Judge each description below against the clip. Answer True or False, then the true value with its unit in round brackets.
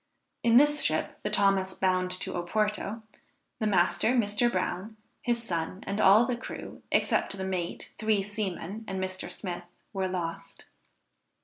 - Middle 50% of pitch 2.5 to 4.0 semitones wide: True (2.9 semitones)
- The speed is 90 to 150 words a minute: True (145 wpm)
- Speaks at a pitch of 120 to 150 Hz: False (195 Hz)